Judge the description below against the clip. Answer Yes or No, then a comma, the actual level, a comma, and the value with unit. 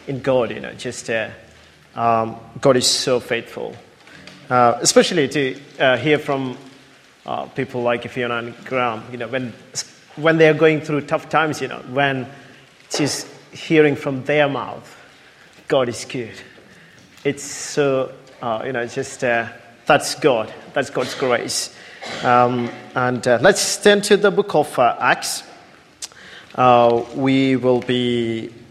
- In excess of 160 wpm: No, average, 145 wpm